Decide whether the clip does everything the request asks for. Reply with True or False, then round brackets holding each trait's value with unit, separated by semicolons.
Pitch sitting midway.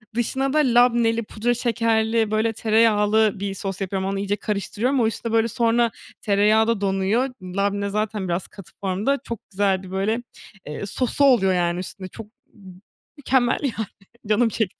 False (215 Hz)